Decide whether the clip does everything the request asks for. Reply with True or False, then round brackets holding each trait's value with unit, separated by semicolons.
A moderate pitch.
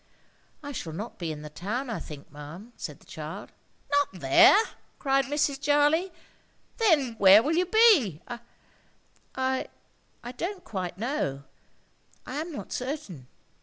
False (255 Hz)